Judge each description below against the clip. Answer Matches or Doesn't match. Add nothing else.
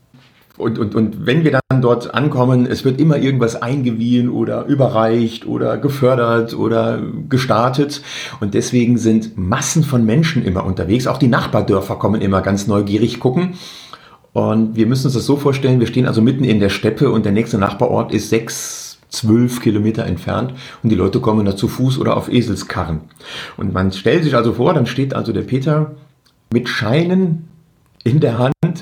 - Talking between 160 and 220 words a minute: Matches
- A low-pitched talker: Matches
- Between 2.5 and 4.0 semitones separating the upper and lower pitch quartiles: Matches